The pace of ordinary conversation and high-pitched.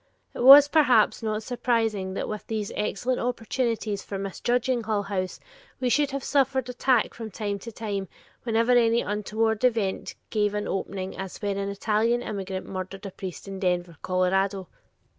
Yes: average, 160 wpm; high, 215 Hz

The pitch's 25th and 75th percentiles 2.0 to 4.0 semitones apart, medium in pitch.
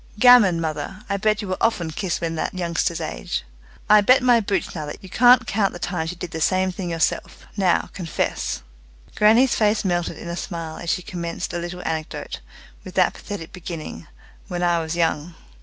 Yes: average, 3.5 semitones; medium, 175 Hz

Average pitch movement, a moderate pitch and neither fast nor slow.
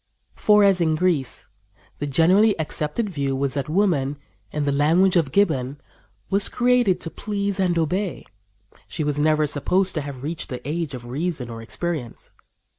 Yes: average, 4.9 semitones; medium, 160 Hz; average, 165 wpm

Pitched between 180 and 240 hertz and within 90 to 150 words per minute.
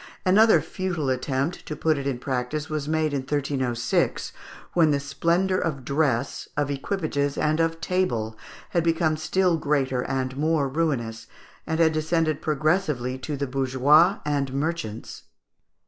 No: medium, 150 Hz; average, 145 wpm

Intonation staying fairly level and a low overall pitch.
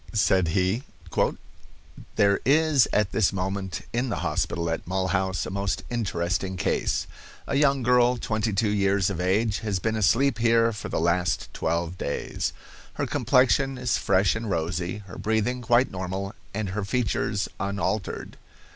No: average, 3.7 semitones; low, 100 Hz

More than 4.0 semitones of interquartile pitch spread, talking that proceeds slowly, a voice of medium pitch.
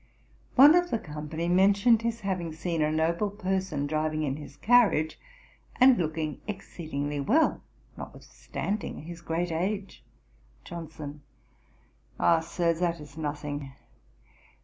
Yes: average, 4.4 semitones; slow, 120 wpm; medium, 170 Hz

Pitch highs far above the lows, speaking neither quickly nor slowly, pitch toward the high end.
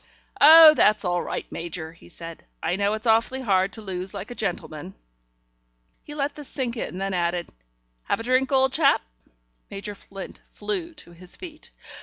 Yes: wide, 6.9 semitones; average, 175 wpm; high, 210 Hz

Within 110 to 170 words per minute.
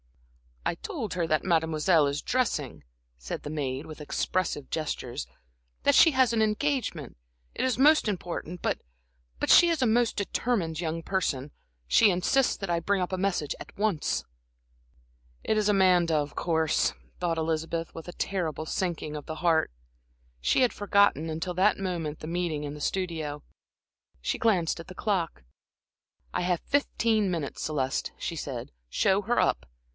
Yes: average, 160 wpm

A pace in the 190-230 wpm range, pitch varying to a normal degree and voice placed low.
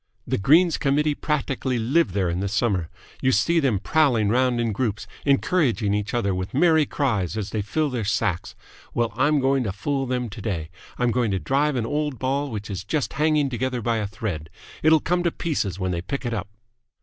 No: fast, 205 wpm; wide, 5.8 semitones; low, 125 Hz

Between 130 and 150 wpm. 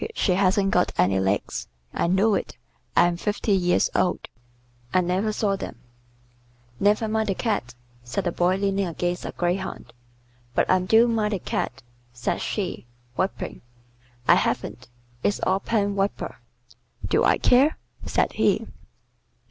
Yes: average, 145 wpm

